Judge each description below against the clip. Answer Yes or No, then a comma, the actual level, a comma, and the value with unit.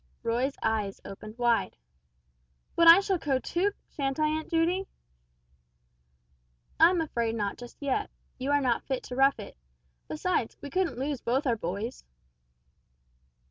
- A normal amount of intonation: No, wide, 5.8 semitones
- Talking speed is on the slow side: No, average, 145 wpm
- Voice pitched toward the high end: Yes, very high, 270 Hz